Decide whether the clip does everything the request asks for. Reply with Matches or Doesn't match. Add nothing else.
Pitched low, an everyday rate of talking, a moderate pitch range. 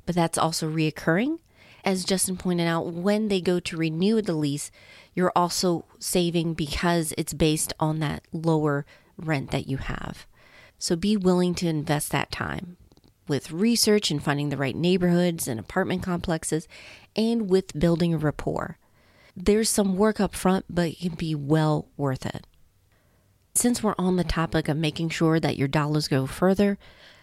Doesn't match